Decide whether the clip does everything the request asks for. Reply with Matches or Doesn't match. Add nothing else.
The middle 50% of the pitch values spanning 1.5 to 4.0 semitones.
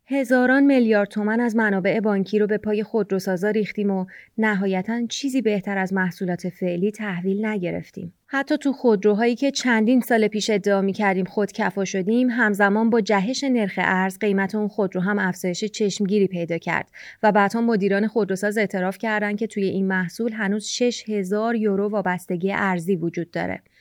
Matches